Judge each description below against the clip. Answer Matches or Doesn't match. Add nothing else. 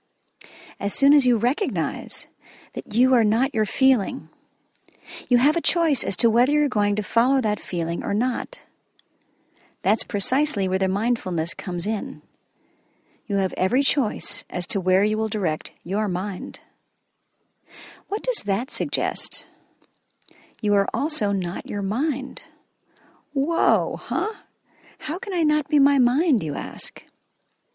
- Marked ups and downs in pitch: Matches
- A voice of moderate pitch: Doesn't match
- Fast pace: Doesn't match